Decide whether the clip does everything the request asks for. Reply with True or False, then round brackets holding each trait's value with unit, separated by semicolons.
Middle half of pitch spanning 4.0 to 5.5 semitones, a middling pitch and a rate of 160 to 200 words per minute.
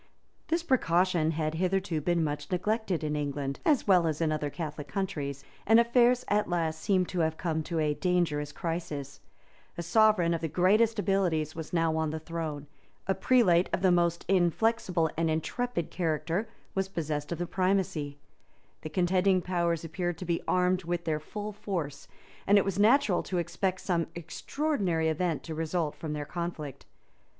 False (3.3 semitones; 170 Hz; 170 wpm)